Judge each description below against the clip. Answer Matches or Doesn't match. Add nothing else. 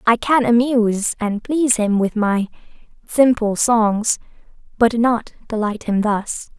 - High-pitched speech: Matches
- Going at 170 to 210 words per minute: Doesn't match